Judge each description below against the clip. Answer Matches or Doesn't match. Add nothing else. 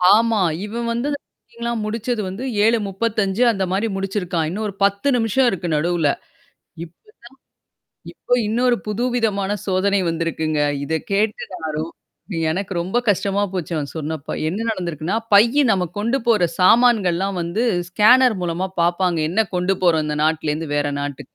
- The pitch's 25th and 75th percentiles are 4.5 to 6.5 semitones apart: Matches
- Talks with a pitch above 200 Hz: Doesn't match